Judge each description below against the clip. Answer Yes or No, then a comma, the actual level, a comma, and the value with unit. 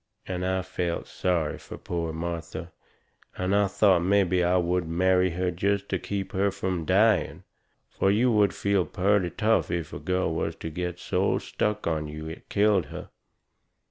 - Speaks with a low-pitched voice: Yes, very low, 90 Hz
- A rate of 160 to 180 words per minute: Yes, average, 170 wpm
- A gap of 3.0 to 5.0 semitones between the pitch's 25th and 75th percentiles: No, narrow, 2.6 semitones